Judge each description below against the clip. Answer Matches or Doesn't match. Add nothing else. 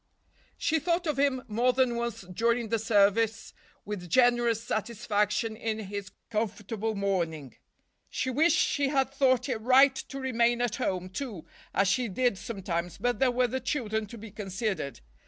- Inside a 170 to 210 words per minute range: Doesn't match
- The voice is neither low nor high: Doesn't match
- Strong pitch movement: Doesn't match